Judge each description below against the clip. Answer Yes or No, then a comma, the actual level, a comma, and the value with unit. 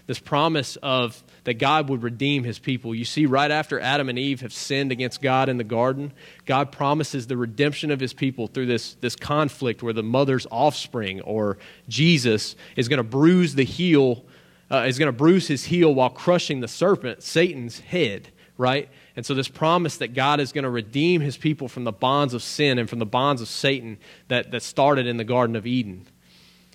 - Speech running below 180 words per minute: No, fast, 205 wpm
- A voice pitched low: Yes, low, 130 Hz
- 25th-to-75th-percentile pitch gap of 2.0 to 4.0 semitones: Yes, average, 3.3 semitones